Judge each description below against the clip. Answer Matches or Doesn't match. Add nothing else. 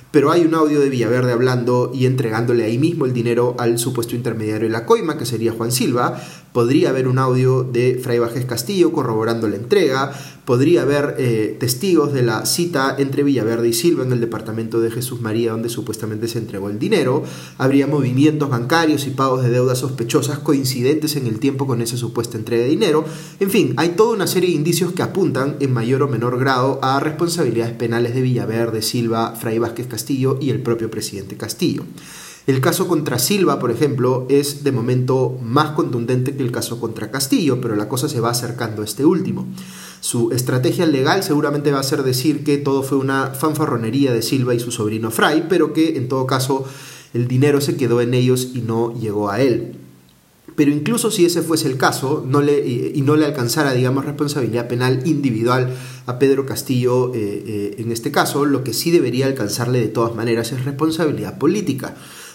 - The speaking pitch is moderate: Doesn't match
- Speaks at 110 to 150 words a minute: Doesn't match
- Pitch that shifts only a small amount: Doesn't match